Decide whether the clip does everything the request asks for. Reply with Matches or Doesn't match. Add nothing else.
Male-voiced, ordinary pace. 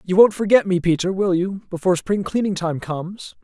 Doesn't match